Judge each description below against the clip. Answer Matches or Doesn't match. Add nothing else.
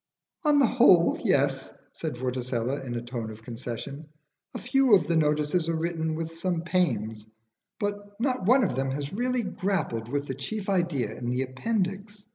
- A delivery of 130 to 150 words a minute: Doesn't match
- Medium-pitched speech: Matches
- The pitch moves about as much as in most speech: Doesn't match